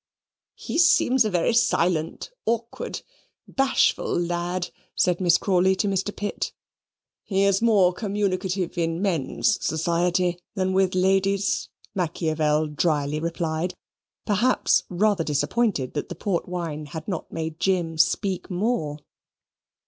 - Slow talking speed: Yes, slow, 120 wpm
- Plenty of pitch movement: No, average, 3.3 semitones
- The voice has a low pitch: No, medium, 180 Hz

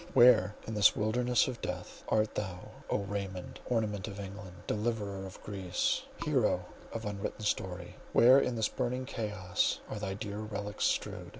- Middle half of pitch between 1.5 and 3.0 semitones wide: Yes, narrow, 2.5 semitones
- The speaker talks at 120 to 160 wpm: Yes, average, 155 wpm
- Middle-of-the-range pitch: No, low, 105 Hz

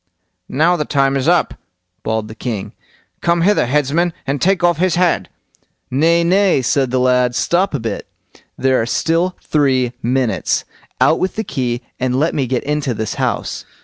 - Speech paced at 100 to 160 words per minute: No, average, 175 wpm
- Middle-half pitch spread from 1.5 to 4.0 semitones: No, average, 5.2 semitones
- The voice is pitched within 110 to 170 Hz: Yes, medium, 140 Hz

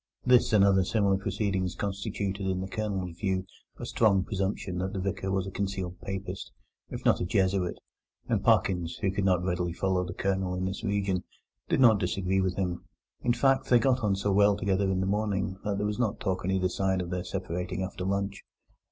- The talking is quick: Yes, fast, 210 wpm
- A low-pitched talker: Yes, very low, 95 Hz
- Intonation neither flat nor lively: No, narrow, 1.5 semitones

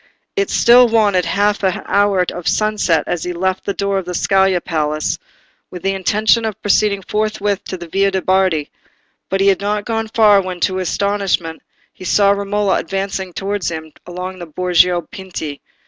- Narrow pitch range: Yes, narrow, 2.3 semitones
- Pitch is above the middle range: Yes, high, 195 Hz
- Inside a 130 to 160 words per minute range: No, average, 180 wpm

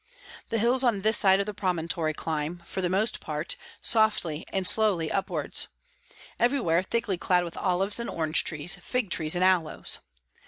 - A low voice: No, medium, 185 Hz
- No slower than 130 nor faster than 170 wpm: Yes, average, 165 wpm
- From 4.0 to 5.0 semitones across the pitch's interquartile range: Yes, average, 4.6 semitones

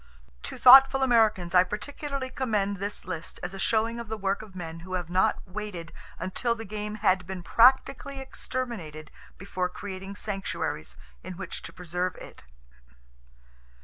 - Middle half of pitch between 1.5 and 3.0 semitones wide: No, average, 4.2 semitones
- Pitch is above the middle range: Yes, high, 200 Hz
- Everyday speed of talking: Yes, average, 150 wpm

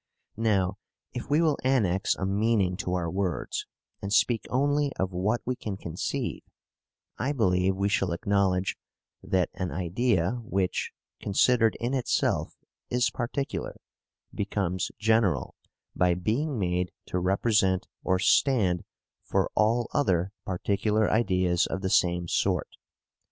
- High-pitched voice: No, low, 100 Hz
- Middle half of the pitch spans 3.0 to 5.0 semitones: Yes, average, 4.3 semitones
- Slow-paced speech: Yes, slow, 130 wpm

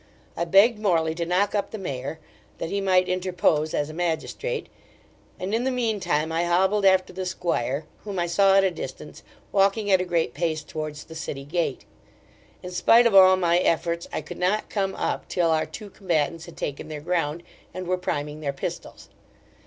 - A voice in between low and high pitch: Yes, medium, 175 Hz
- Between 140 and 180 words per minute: No, average, 195 wpm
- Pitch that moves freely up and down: No, average, 3.4 semitones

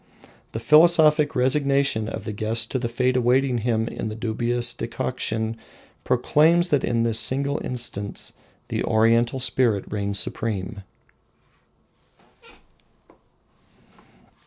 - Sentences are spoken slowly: Yes, slow, 110 wpm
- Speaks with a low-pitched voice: Yes, low, 120 Hz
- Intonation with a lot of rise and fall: No, average, 3.3 semitones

